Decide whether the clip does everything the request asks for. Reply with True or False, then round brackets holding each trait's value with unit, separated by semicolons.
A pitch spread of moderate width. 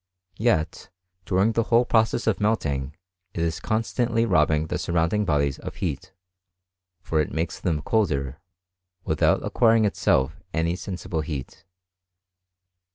False (6.2 semitones)